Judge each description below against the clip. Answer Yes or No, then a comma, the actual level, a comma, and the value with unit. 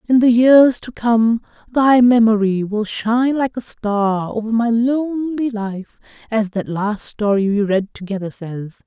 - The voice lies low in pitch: No, high, 225 Hz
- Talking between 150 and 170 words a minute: Yes, average, 160 wpm